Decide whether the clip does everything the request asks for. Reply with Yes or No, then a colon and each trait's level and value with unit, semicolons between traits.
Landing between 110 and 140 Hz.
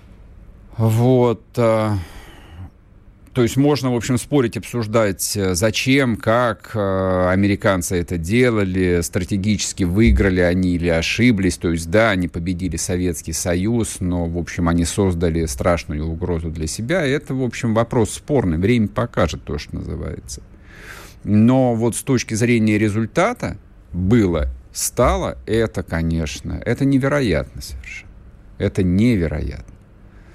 No: low, 100 Hz